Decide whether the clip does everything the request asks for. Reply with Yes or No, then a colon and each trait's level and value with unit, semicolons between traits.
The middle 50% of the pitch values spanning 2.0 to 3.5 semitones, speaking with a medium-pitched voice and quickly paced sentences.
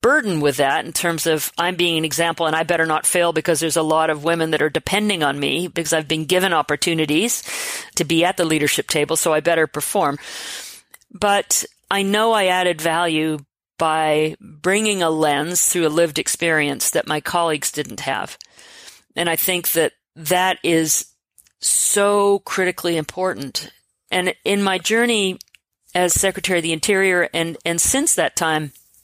No: average, 2.9 semitones; medium, 170 Hz; average, 170 wpm